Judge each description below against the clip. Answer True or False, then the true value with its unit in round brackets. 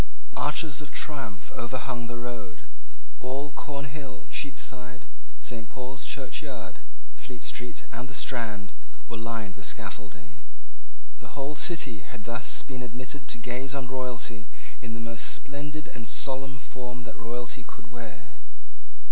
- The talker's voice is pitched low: True (125 Hz)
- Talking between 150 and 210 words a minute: False (140 wpm)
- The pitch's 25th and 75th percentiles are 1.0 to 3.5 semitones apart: True (2.8 semitones)